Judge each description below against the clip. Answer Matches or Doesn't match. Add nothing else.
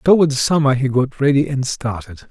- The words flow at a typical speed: Matches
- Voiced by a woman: Doesn't match